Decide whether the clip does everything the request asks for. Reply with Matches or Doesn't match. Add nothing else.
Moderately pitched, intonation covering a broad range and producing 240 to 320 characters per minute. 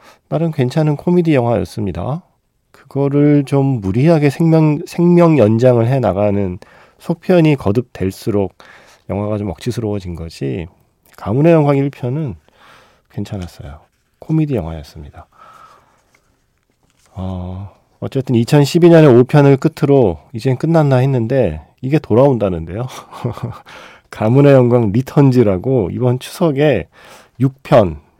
Doesn't match